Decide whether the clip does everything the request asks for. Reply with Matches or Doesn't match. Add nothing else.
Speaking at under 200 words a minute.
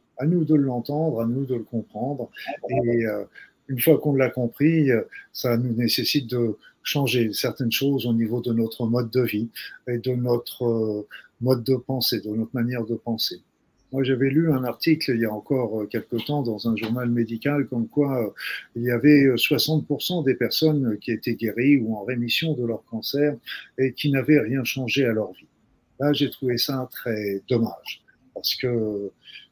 Matches